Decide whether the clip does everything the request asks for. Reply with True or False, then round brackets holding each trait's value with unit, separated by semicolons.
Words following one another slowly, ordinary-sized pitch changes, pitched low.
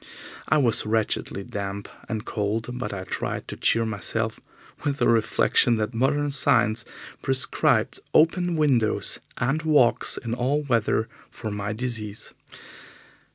True (130 wpm; 3.9 semitones; 115 Hz)